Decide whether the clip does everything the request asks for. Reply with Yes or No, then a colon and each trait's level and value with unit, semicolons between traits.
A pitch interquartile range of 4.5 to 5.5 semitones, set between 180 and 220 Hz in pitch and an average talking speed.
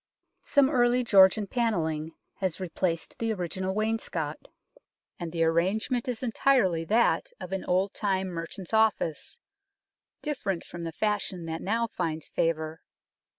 No: average, 5.1 semitones; high, 190 Hz; slow, 130 wpm